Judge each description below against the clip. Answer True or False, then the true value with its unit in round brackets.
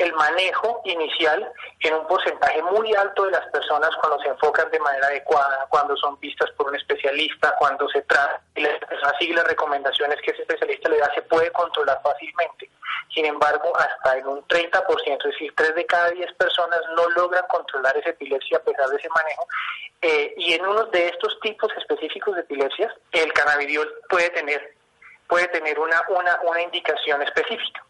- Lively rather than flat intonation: True (6.4 semitones)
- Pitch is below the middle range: False (175 Hz)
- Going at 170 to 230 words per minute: True (180 wpm)